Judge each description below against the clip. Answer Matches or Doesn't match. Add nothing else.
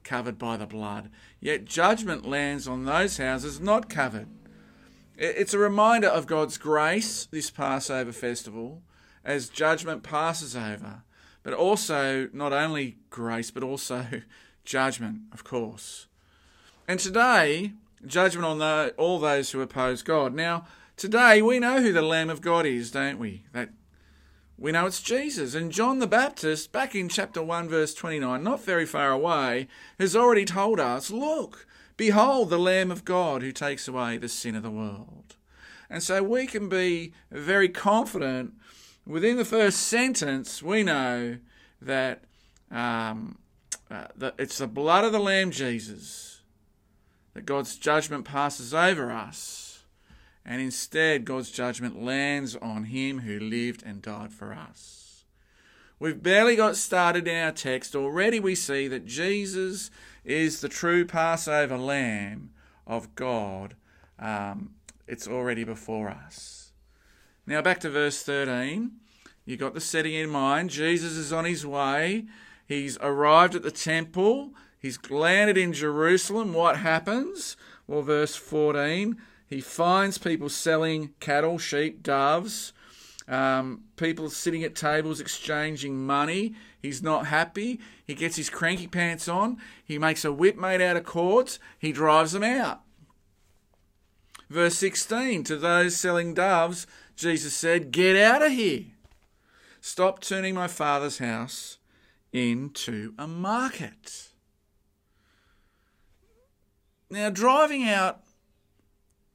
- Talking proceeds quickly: Doesn't match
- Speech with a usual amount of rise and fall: Doesn't match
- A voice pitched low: Doesn't match